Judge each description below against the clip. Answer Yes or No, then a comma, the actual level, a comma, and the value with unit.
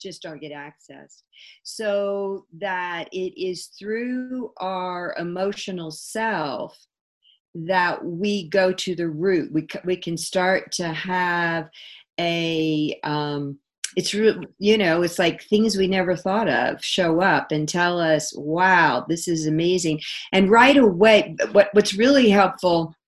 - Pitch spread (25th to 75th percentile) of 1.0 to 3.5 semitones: Yes, average, 3.2 semitones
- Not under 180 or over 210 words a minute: No, average, 140 wpm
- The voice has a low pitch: No, medium, 180 Hz